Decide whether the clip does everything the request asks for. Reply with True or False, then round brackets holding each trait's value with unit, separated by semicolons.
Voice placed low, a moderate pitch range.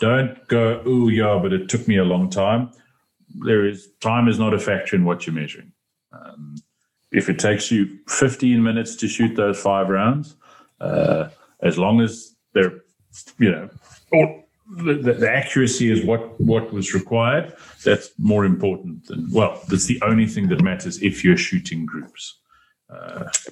True (115 Hz; 4.2 semitones)